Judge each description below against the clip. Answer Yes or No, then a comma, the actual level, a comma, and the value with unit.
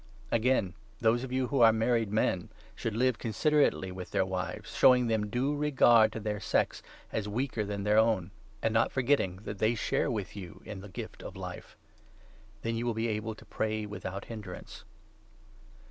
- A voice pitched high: No, low, 110 Hz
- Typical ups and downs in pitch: Yes, average, 3.0 semitones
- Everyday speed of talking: Yes, average, 180 wpm